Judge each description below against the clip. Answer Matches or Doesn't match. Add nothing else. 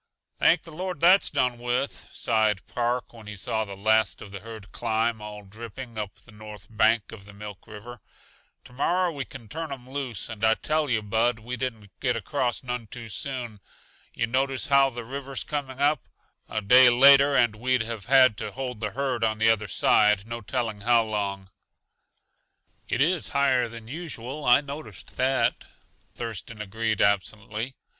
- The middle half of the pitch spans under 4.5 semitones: Matches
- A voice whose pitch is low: Matches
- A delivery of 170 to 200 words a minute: Matches